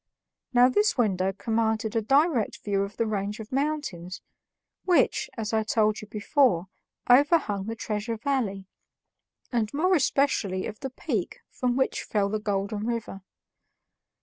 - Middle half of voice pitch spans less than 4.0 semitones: No, average, 4.3 semitones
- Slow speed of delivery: No, average, 145 wpm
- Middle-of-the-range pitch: No, high, 220 Hz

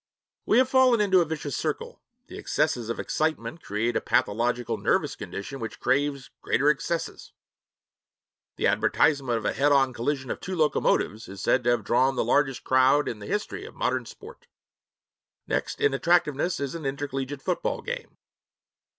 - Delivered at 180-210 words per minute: No, average, 165 wpm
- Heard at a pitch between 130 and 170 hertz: Yes, medium, 140 Hz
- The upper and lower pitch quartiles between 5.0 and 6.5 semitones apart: Yes, wide, 5.5 semitones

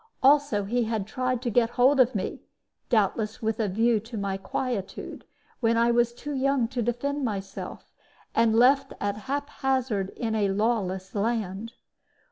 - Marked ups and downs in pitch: No, average, 3.5 semitones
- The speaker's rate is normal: Yes, average, 155 wpm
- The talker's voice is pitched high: Yes, high, 230 Hz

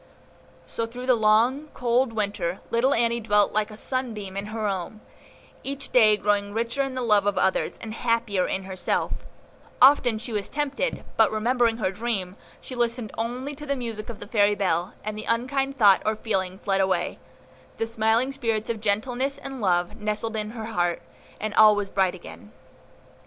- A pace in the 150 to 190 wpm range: Yes, average, 180 wpm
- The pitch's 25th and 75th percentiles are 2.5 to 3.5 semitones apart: Yes, average, 3.0 semitones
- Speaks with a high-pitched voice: Yes, high, 220 Hz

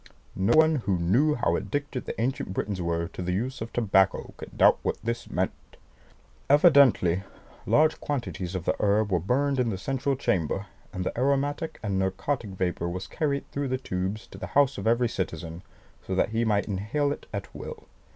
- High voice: No, low, 110 Hz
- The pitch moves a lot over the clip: Yes, wide, 6.7 semitones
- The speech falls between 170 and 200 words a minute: Yes, average, 190 wpm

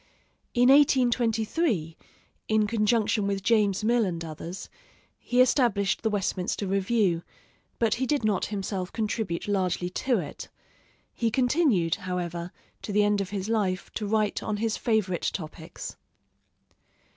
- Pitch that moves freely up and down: No, average, 3.7 semitones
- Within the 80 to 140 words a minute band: Yes, slow, 135 wpm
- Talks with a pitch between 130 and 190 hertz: No, high, 210 Hz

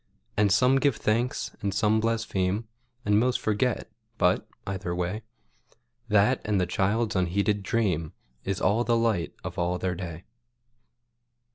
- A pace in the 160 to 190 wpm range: No, average, 140 wpm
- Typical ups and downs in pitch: Yes, average, 3.8 semitones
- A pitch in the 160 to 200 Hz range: No, low, 105 Hz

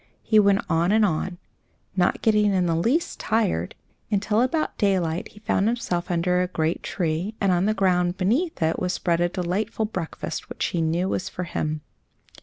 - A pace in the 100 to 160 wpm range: No, average, 185 wpm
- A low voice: No, medium, 185 Hz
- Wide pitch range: No, average, 3.4 semitones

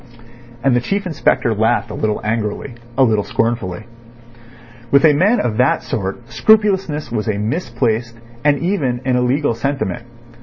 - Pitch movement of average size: Yes, average, 5.0 semitones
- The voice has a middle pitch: No, low, 120 Hz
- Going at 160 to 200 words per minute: No, average, 150 wpm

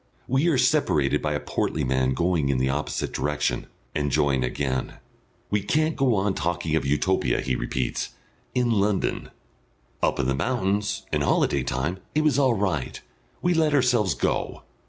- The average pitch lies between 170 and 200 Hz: No, very low, 95 Hz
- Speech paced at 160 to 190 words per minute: Yes, average, 165 wpm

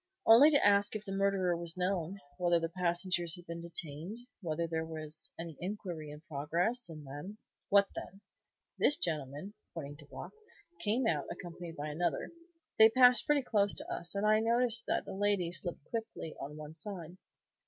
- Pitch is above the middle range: No, medium, 175 Hz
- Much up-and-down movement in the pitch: No, average, 4.1 semitones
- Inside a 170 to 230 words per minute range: Yes, average, 180 wpm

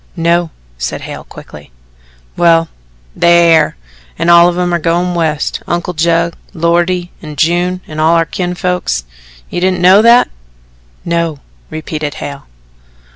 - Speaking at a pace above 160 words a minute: No, slow, 135 wpm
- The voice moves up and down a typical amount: No, narrow, 1.7 semitones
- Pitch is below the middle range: No, medium, 170 Hz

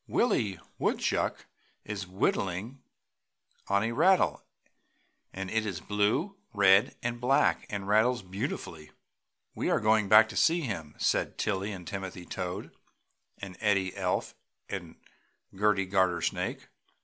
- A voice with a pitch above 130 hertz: No, low, 100 Hz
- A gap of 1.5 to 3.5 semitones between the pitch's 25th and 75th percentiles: Yes, average, 2.8 semitones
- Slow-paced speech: Yes, slow, 125 wpm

